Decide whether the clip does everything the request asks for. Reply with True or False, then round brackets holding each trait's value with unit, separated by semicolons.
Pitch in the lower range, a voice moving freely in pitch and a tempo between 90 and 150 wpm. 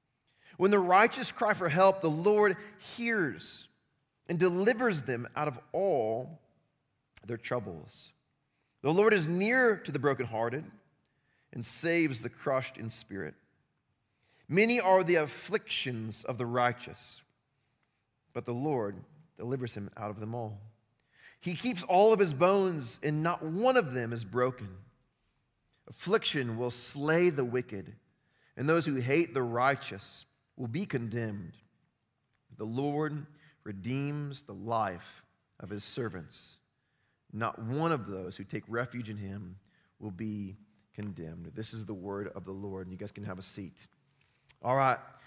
True (130 Hz; 6.1 semitones; 145 wpm)